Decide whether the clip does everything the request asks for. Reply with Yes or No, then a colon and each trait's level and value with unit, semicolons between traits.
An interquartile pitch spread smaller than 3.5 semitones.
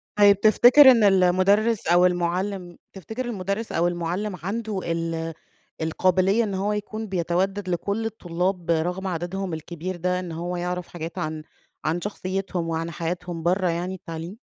Yes: average, 2.7 semitones